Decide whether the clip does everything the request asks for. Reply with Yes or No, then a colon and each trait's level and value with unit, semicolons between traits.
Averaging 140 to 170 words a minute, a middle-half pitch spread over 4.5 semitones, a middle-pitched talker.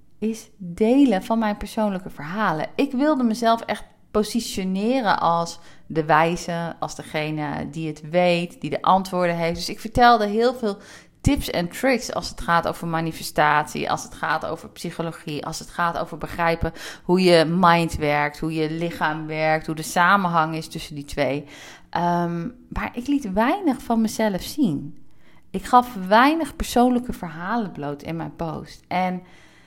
Yes: average, 160 wpm; average, 5.3 semitones; medium, 175 Hz